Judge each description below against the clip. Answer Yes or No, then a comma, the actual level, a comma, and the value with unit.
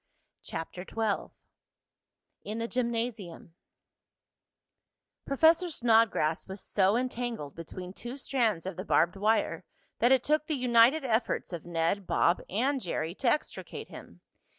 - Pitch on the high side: Yes, high, 225 Hz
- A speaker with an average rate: No, slow, 130 wpm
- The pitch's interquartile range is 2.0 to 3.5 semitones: No, average, 5.3 semitones